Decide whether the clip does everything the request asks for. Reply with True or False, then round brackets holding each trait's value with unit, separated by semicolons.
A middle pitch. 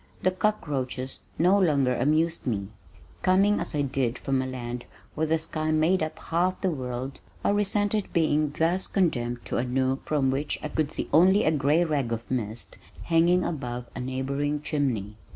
True (150 Hz)